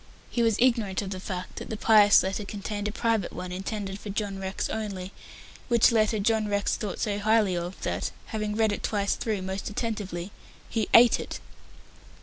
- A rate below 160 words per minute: No, average, 185 wpm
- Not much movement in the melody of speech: Yes, narrow, 2.3 semitones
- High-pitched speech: Yes, high, 205 Hz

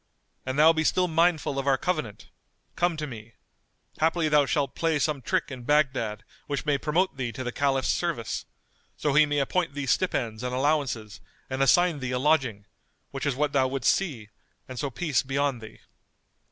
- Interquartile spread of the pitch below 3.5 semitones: Yes, average, 3.1 semitones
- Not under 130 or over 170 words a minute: No, average, 190 wpm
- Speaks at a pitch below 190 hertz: Yes, medium, 140 Hz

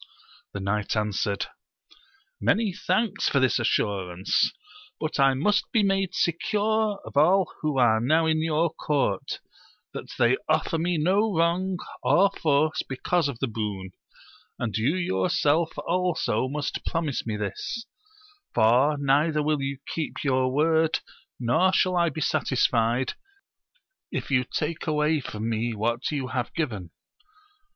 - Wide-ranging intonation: Yes, wide, 6.0 semitones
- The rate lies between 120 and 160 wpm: Yes, average, 140 wpm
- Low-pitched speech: No, medium, 145 Hz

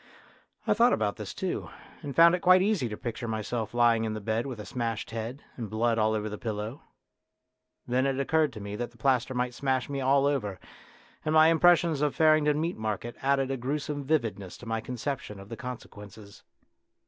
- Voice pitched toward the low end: Yes, low, 125 Hz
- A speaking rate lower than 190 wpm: No, fast, 205 wpm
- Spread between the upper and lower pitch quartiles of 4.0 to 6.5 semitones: Yes, average, 4.6 semitones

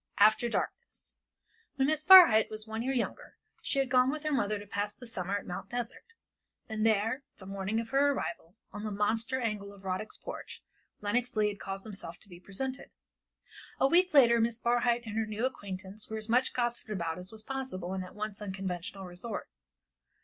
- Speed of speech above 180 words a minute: Yes, average, 195 wpm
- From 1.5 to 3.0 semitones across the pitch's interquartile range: No, average, 3.7 semitones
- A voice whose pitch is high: Yes, high, 220 Hz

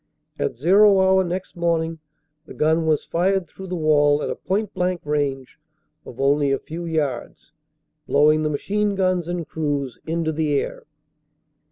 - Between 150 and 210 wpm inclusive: Yes, average, 160 wpm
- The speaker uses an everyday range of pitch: Yes, average, 3.8 semitones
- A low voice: No, medium, 160 Hz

